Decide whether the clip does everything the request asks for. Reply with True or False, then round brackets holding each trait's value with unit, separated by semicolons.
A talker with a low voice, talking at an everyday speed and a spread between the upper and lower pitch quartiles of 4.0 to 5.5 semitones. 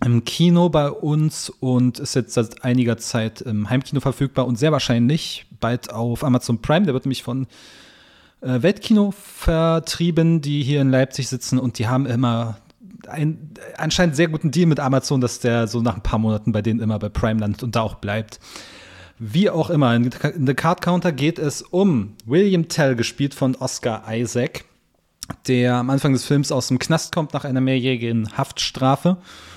True (130 Hz; 180 wpm; 4.5 semitones)